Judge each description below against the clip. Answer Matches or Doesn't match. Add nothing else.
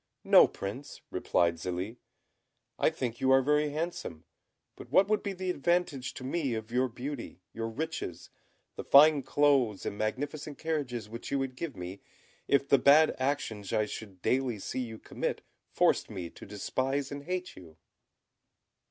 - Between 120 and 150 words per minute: Doesn't match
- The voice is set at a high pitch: Doesn't match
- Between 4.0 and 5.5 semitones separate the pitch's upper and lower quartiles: Matches